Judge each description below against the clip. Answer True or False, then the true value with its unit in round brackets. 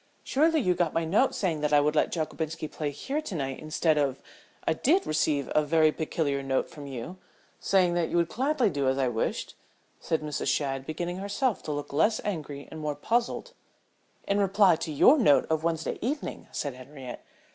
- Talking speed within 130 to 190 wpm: False (200 wpm)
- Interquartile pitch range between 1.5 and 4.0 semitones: False (5.0 semitones)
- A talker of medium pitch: True (160 Hz)